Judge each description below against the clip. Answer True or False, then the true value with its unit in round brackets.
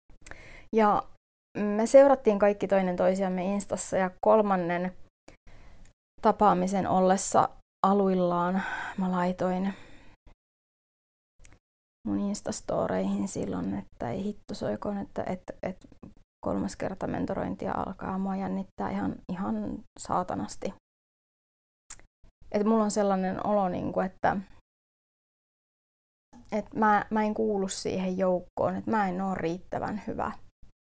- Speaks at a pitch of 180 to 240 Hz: True (190 Hz)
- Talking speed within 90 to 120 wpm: True (100 wpm)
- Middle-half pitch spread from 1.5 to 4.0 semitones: True (2.9 semitones)